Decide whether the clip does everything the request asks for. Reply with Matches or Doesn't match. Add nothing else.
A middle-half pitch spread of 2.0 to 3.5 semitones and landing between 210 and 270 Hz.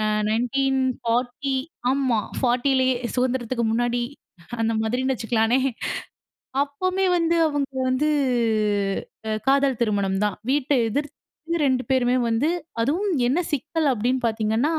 Matches